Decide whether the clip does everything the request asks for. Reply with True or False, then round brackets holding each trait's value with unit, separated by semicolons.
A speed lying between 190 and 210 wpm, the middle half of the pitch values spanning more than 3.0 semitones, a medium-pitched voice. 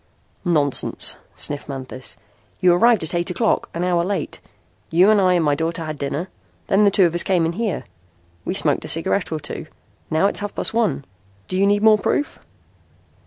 True (195 wpm; 3.8 semitones; 180 Hz)